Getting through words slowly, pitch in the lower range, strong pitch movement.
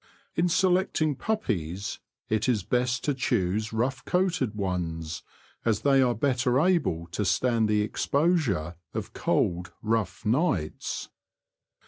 Yes: slow, 120 wpm; low, 115 Hz; wide, 6.8 semitones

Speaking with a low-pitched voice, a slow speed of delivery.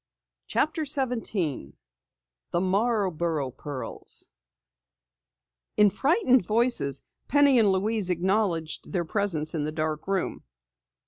No: high, 190 Hz; slow, 100 wpm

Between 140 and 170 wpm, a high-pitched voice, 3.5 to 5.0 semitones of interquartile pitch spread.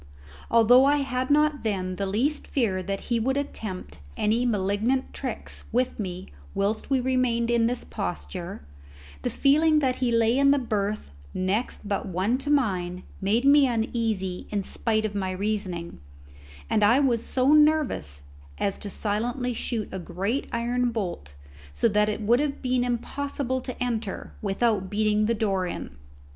Yes: average, 160 wpm; high, 225 Hz; average, 4.3 semitones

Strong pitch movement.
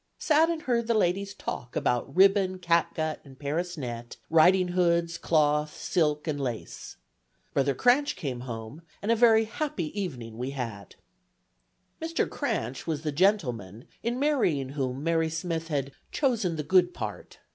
Yes: wide, 6.2 semitones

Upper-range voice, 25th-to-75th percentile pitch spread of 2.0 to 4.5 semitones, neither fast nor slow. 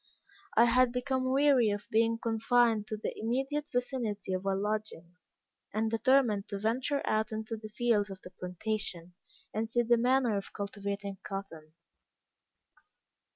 Yes: high, 220 Hz; average, 3.3 semitones; average, 145 wpm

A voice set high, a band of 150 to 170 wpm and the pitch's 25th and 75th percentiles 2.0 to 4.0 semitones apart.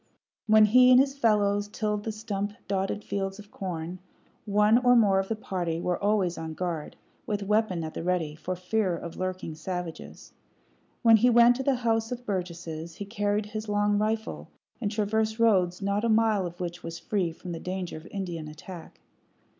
No: high, 200 Hz; average, 185 wpm; average, 3.5 semitones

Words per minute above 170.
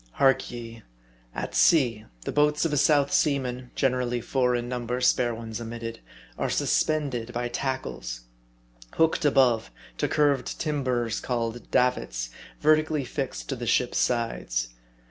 No: average, 140 wpm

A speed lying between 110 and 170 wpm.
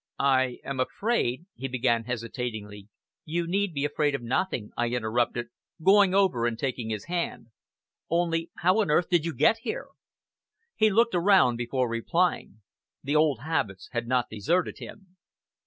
Yes: average, 155 wpm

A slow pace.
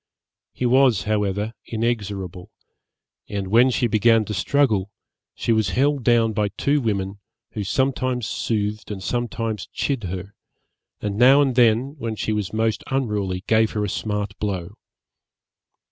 No: average, 145 wpm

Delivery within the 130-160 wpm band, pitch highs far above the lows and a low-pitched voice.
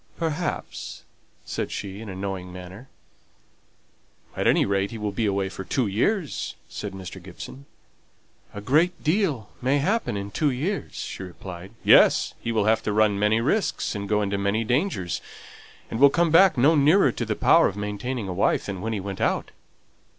No: average, 180 wpm; wide, 6.1 semitones; low, 105 Hz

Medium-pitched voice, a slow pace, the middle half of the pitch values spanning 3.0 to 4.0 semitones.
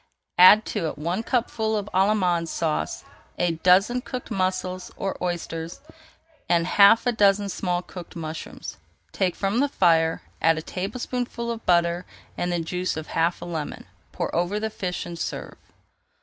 No: medium, 180 Hz; average, 160 wpm; average, 3.5 semitones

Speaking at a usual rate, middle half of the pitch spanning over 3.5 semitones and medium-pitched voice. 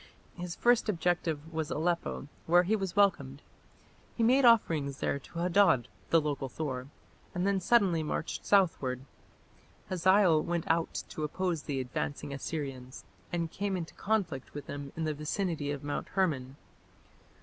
Yes: average, 150 wpm; average, 4.6 semitones; medium, 165 Hz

